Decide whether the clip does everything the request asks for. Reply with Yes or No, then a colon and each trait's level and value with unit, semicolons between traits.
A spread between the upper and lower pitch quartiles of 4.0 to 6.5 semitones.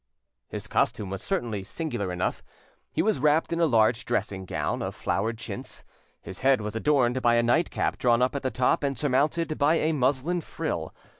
Yes: average, 5.0 semitones